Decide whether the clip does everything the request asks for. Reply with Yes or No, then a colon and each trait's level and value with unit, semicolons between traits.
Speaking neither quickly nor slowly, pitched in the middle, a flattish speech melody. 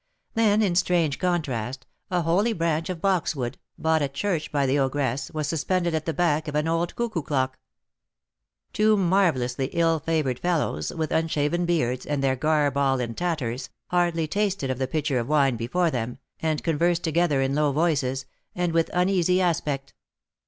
No: average, 170 wpm; medium, 155 Hz; average, 4.2 semitones